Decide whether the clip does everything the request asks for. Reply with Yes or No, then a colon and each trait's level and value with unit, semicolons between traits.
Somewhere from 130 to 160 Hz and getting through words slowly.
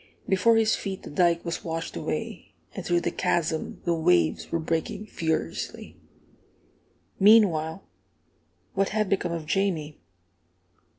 No: medium, 170 Hz; slow, 125 wpm